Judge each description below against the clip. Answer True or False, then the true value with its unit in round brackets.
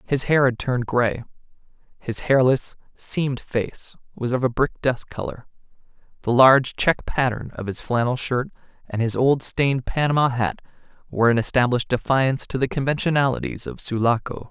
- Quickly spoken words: False (155 wpm)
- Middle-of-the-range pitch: False (130 Hz)